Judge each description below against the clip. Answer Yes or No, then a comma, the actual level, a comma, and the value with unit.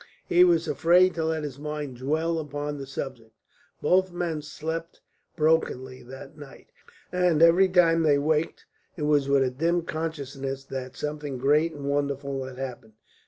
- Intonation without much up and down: No, average, 3.3 semitones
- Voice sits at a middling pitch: Yes, medium, 150 Hz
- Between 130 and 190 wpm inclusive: Yes, average, 160 wpm